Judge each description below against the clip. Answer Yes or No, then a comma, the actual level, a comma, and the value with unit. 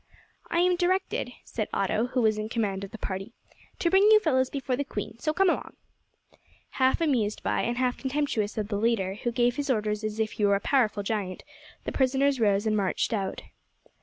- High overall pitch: Yes, high, 230 Hz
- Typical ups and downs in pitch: Yes, average, 4.6 semitones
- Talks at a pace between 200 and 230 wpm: Yes, fast, 205 wpm